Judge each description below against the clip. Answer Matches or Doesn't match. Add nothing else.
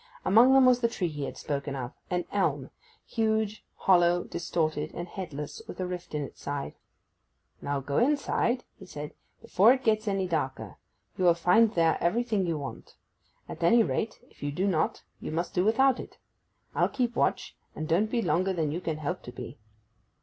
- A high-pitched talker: Doesn't match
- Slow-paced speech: Doesn't match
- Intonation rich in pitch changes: Matches